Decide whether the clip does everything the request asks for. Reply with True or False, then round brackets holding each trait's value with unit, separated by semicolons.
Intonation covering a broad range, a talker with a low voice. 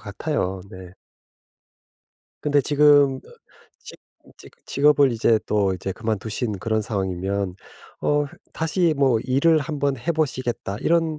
True (6.4 semitones; 130 Hz)